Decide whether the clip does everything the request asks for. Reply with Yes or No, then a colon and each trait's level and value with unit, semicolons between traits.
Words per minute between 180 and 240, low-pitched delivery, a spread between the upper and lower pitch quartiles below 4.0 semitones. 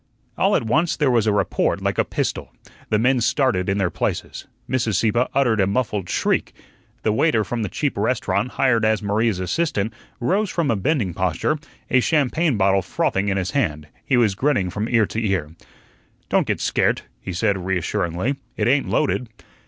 No: average, 185 wpm; low, 110 Hz; average, 4.9 semitones